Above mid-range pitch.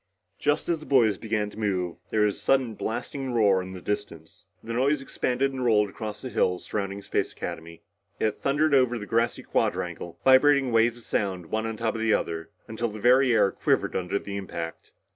No: low, 110 Hz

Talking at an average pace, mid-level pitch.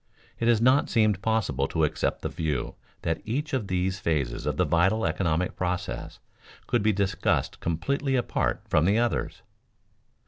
No: average, 160 wpm; very low, 95 Hz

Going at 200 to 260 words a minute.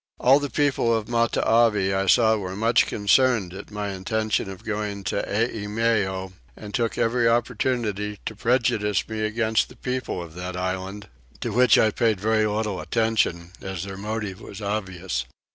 No: average, 160 wpm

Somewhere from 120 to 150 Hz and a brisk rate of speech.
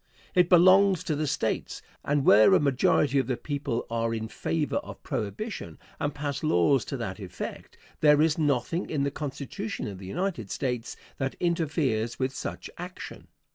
No: medium, 140 Hz; average, 170 wpm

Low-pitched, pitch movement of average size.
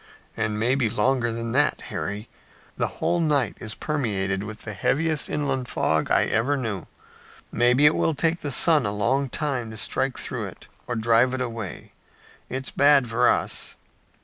Yes: low, 125 Hz; average, 4.4 semitones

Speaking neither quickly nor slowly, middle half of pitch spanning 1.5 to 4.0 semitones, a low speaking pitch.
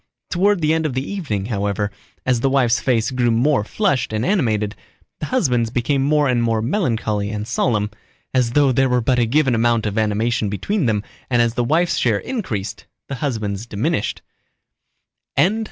No: average, 175 wpm; average, 4.5 semitones; low, 120 Hz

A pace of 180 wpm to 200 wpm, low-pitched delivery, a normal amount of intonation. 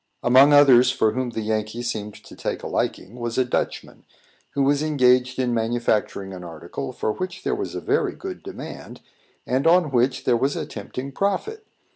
Yes: average, 185 wpm; low, 125 Hz; average, 4.1 semitones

